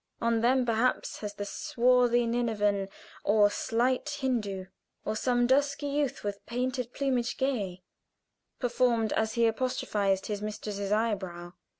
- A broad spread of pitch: No, average, 3.5 semitones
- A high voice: Yes, high, 230 Hz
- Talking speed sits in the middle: No, slow, 125 wpm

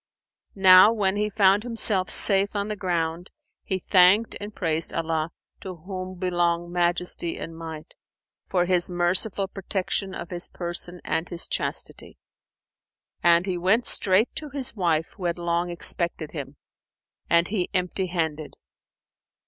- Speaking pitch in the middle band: Yes, medium, 180 Hz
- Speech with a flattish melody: Yes, narrow, 2.3 semitones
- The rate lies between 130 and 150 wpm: Yes, average, 140 wpm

